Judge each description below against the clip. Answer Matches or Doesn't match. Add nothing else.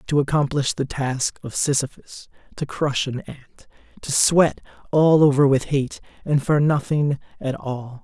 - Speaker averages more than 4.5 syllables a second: Doesn't match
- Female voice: Doesn't match